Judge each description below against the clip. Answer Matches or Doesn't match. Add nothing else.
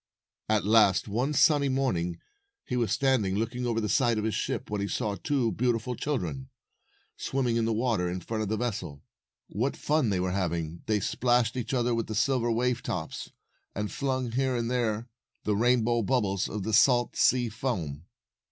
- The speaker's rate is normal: Matches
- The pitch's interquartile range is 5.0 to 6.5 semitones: Doesn't match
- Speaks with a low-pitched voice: Matches